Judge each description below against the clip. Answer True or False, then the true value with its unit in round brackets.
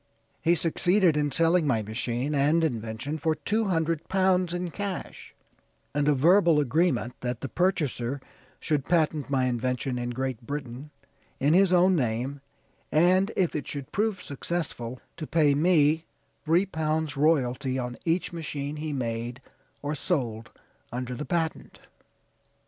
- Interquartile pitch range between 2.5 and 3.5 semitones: False (4.9 semitones)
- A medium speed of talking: True (145 wpm)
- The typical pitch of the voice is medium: True (150 Hz)